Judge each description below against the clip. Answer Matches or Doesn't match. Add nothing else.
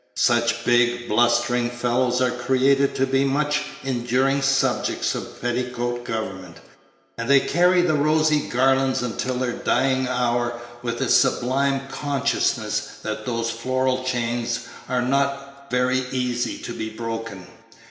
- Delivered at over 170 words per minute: Doesn't match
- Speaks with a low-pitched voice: Matches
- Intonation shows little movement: Matches